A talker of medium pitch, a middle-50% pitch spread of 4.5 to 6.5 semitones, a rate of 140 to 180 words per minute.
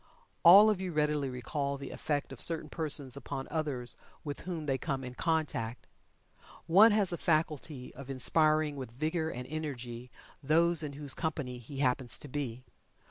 No: medium, 145 Hz; average, 3.5 semitones; average, 165 wpm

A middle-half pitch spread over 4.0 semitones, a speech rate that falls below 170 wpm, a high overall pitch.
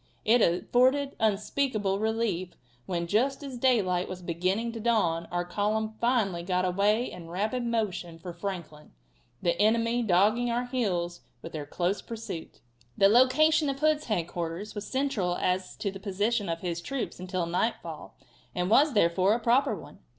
Yes: average, 5.0 semitones; average, 160 wpm; high, 205 Hz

